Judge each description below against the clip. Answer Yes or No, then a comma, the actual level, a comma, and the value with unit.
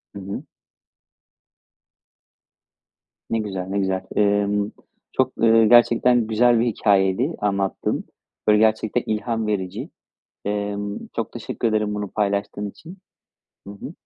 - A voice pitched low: Yes, low, 105 Hz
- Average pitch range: No, narrow, 2.0 semitones